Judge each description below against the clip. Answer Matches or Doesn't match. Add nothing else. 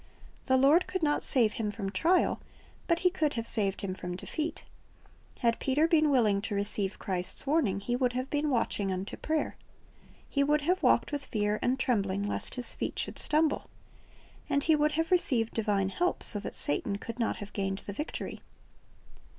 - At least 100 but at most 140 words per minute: Doesn't match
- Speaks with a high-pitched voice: Matches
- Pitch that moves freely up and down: Matches